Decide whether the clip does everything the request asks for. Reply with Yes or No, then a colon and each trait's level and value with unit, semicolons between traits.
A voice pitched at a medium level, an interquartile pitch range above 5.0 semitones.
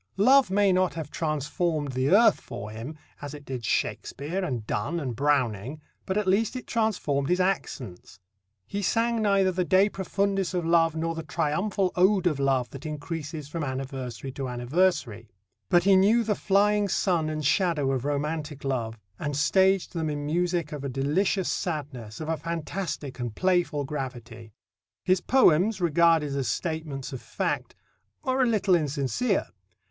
Yes: medium, 160 Hz; wide, 5.5 semitones